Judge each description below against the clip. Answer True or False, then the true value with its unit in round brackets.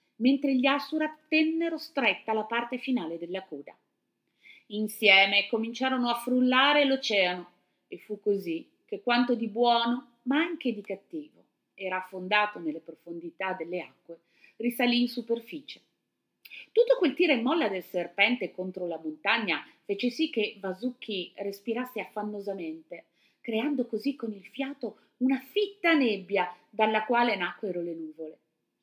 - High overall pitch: True (220 Hz)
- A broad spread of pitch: True (5.7 semitones)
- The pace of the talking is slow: False (135 wpm)